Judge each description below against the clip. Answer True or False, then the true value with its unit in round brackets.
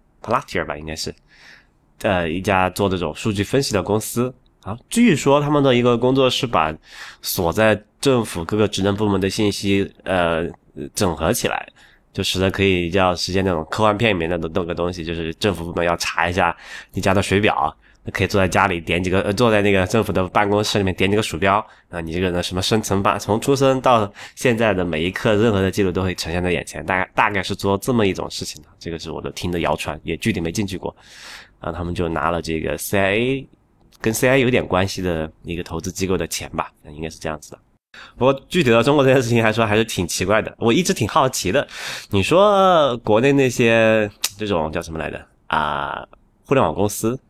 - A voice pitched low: True (100 Hz)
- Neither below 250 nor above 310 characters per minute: False (325 characters per minute)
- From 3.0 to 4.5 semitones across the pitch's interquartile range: True (4.2 semitones)